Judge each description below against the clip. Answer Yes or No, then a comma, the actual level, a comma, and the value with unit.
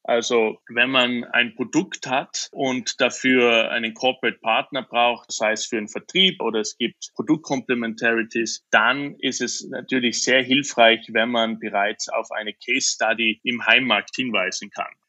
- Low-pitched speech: Yes, low, 120 Hz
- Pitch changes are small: Yes, narrow, 2.3 semitones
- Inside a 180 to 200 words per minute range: No, average, 150 wpm